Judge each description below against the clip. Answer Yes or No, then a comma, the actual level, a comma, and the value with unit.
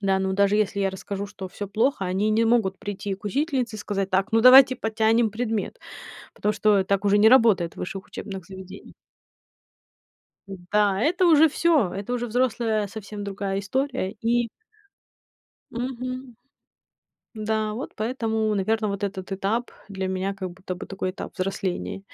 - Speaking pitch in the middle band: No, high, 210 Hz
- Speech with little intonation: No, average, 3.1 semitones